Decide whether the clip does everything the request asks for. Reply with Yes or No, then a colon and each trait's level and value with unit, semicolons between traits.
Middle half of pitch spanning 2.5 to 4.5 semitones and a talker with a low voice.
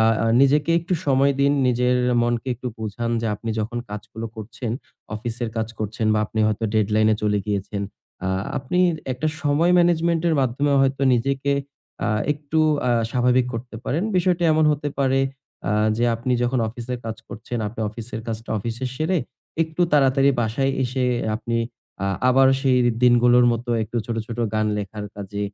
Yes: average, 3.6 semitones; low, 120 Hz